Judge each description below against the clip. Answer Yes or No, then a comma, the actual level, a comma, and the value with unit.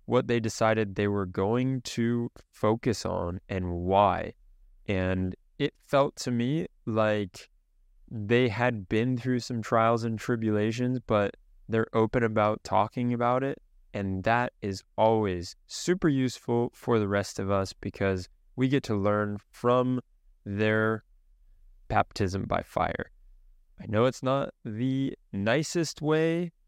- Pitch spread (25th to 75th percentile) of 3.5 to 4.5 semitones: Yes, average, 4.0 semitones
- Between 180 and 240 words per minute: No, slow, 135 wpm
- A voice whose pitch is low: Yes, low, 110 Hz